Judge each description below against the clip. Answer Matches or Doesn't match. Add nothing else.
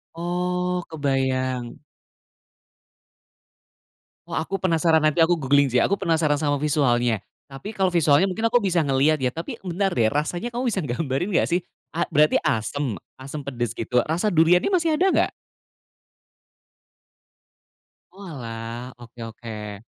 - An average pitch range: Doesn't match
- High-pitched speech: Doesn't match